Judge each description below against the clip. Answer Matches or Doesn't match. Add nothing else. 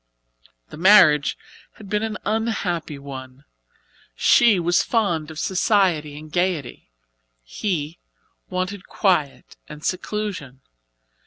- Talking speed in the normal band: Doesn't match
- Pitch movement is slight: Doesn't match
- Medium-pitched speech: Matches